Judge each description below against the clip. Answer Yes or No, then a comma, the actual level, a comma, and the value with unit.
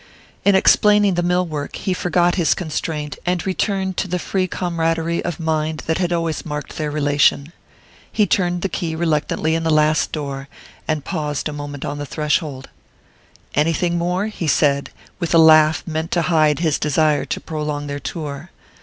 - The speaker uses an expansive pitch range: No, average, 2.8 semitones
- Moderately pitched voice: Yes, medium, 160 Hz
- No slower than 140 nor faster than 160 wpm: No, average, 175 wpm